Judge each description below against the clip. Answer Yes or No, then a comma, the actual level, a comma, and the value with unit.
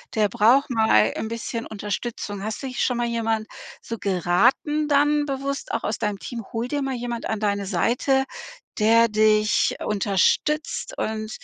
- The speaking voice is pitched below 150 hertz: No, high, 230 Hz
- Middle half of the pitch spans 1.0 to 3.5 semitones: No, average, 3.9 semitones